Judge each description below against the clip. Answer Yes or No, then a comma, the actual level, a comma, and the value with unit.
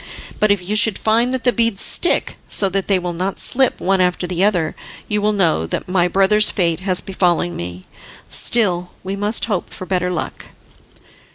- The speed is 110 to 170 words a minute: No, average, 190 wpm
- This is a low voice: No, high, 190 Hz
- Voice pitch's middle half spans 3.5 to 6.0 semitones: No, average, 2.9 semitones